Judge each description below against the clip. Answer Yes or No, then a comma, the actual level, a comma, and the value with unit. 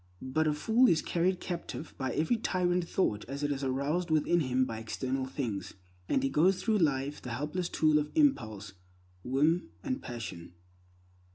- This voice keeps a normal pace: Yes, average, 170 wpm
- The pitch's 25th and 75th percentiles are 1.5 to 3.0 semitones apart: No, wide, 5.4 semitones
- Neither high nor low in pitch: Yes, medium, 150 Hz